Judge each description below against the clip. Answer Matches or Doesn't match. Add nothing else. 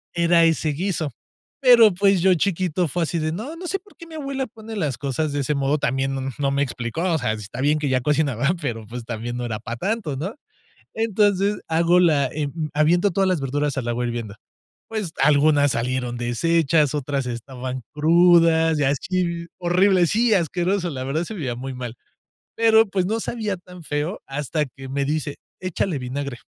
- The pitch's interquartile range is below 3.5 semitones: Doesn't match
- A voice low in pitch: Doesn't match